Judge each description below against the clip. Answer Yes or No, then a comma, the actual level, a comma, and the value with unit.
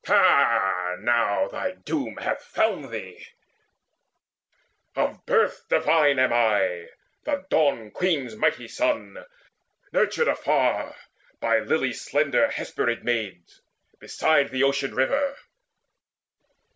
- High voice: No, low, 130 Hz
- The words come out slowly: Yes, slow, 100 wpm